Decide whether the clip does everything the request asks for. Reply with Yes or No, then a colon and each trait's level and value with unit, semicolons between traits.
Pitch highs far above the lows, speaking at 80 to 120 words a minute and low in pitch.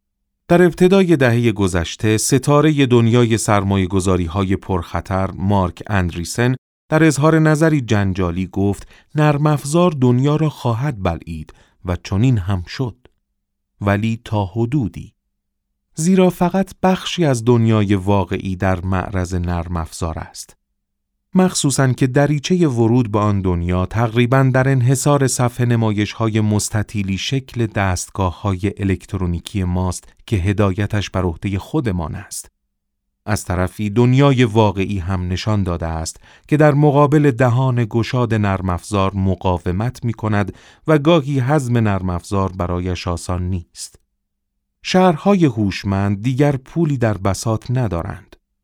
Yes: wide, 6.1 semitones; average, 115 wpm; low, 105 Hz